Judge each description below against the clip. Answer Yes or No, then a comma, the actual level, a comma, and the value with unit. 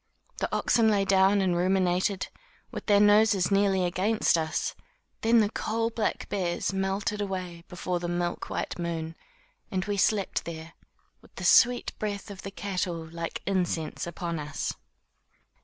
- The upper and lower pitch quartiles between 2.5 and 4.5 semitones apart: Yes, average, 2.9 semitones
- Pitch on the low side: No, high, 190 Hz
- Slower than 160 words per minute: Yes, average, 150 wpm